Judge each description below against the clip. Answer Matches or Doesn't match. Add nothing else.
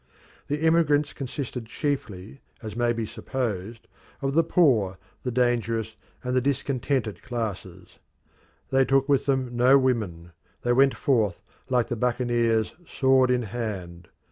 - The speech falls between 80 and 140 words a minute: Matches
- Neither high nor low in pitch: Doesn't match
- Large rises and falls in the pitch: Doesn't match